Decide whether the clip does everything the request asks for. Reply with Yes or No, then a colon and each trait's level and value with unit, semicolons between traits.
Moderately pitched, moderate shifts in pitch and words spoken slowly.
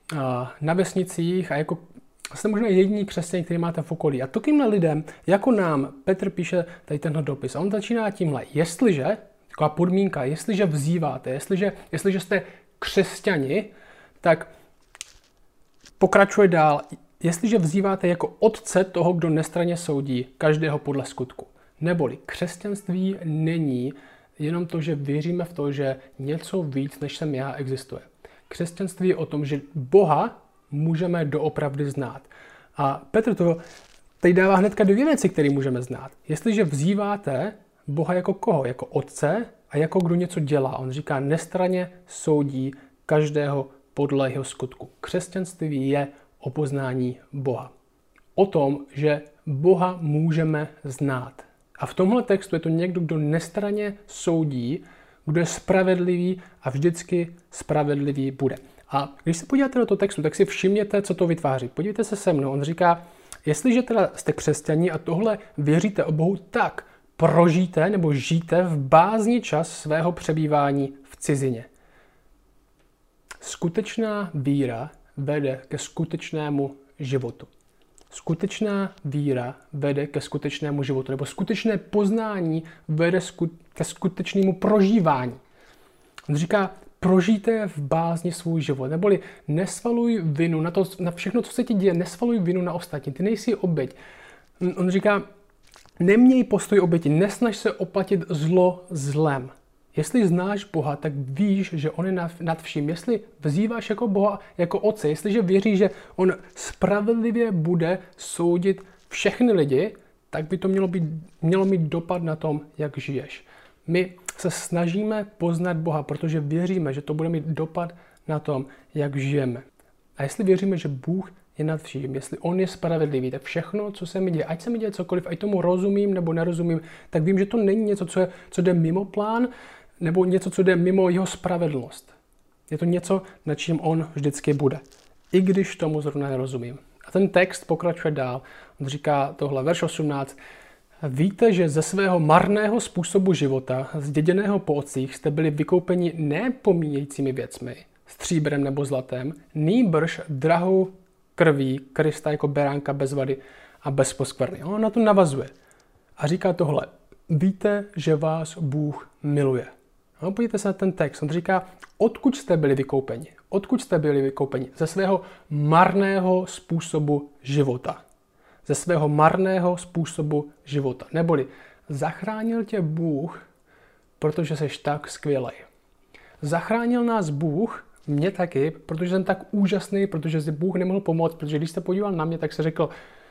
No: medium, 165 Hz; average, 4.5 semitones; average, 145 wpm